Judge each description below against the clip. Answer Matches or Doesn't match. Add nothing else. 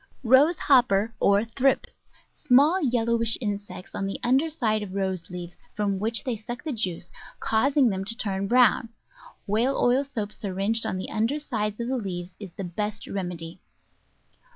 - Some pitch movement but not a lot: Matches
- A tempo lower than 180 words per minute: Matches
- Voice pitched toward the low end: Doesn't match